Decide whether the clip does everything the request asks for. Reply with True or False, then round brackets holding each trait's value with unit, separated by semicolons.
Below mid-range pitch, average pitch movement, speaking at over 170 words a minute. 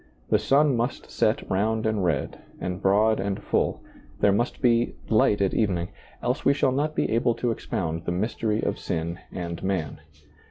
True (105 Hz; 4.5 semitones; 185 wpm)